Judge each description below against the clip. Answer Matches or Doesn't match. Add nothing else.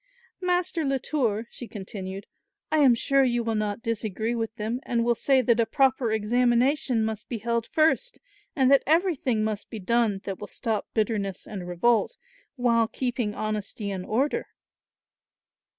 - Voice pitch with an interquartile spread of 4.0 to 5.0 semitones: Doesn't match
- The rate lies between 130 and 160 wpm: Matches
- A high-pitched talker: Matches